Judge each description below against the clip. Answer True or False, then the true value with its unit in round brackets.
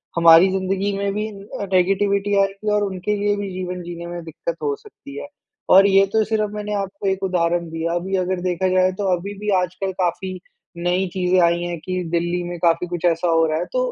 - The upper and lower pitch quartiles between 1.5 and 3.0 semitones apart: True (2.4 semitones)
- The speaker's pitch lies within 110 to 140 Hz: False (185 Hz)